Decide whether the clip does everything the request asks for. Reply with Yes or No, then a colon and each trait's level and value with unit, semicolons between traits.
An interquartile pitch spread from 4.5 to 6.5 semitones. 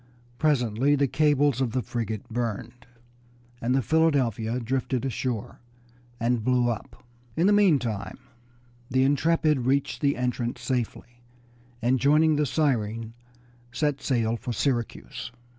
No: average, 3.5 semitones